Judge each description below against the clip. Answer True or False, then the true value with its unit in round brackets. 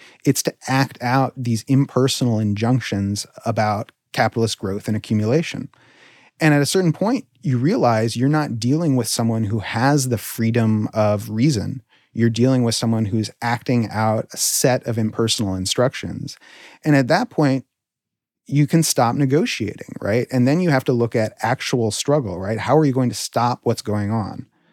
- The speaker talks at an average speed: True (170 wpm)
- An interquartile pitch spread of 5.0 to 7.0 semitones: False (3.6 semitones)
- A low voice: True (120 Hz)